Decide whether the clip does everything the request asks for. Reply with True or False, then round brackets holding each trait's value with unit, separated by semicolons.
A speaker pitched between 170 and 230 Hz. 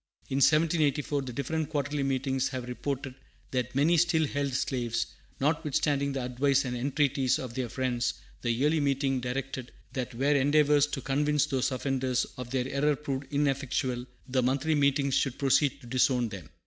False (135 Hz)